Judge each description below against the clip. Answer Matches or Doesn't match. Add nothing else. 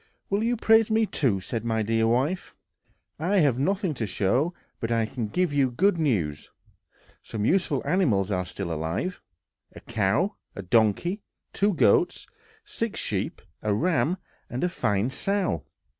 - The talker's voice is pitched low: Matches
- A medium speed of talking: Matches